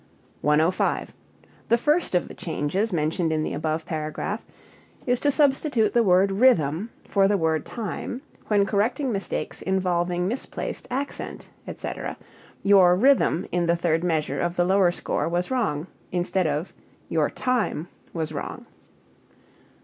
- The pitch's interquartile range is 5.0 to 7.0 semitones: Yes, wide, 5.4 semitones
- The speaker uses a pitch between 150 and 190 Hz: Yes, medium, 185 Hz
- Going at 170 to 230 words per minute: No, average, 140 wpm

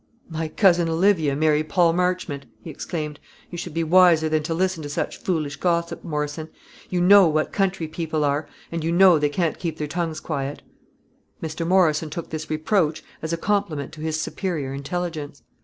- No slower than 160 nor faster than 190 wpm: Yes, average, 180 wpm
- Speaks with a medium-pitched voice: Yes, medium, 160 Hz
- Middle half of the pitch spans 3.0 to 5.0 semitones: No, narrow, 2.5 semitones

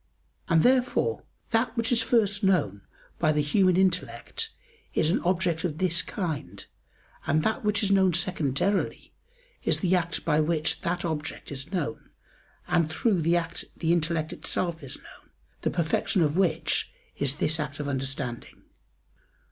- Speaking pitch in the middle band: Yes, medium, 170 Hz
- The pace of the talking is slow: No, average, 155 wpm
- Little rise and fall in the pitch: No, average, 3.8 semitones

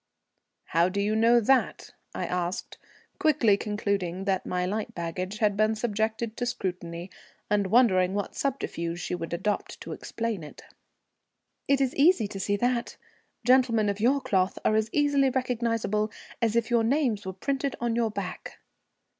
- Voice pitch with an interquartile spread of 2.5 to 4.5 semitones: Yes, average, 4.1 semitones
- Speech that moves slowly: No, average, 160 wpm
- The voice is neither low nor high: No, high, 215 Hz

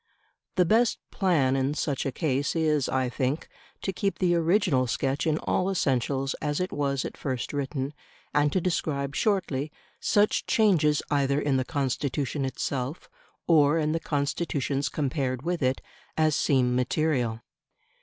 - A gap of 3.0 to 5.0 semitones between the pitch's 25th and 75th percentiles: Yes, average, 3.6 semitones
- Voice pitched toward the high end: No, medium, 145 Hz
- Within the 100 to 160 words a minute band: Yes, average, 150 wpm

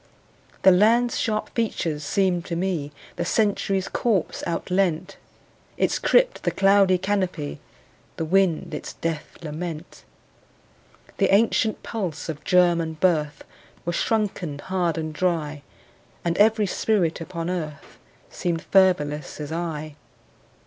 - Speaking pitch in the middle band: Yes, medium, 175 Hz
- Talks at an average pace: No, slow, 120 wpm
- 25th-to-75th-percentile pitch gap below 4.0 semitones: Yes, average, 3.6 semitones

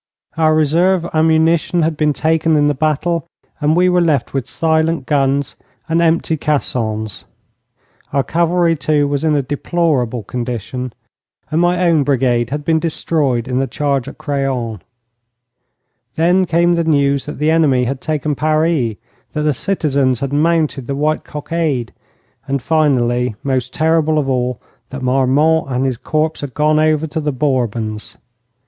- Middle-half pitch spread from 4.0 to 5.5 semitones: No, average, 3.6 semitones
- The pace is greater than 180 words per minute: No, average, 155 wpm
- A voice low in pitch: No, medium, 150 Hz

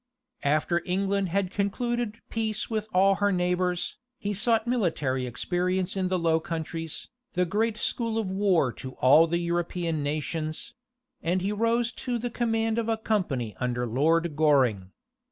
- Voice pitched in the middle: Yes, medium, 180 Hz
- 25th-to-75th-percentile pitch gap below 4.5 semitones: No, average, 5.1 semitones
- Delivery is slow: No, average, 155 wpm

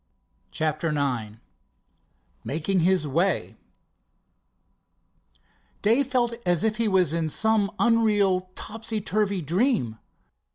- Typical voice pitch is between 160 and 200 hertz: Yes, high, 190 Hz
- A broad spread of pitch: Yes, wide, 5.7 semitones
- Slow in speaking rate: Yes, slow, 95 wpm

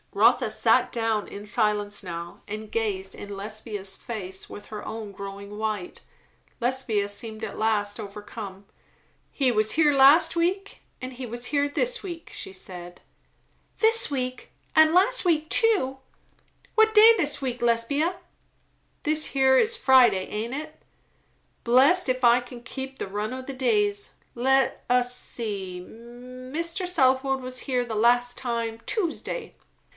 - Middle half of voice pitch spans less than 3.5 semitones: No, average, 5.3 semitones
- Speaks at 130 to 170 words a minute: Yes, average, 145 wpm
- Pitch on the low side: No, high, 245 Hz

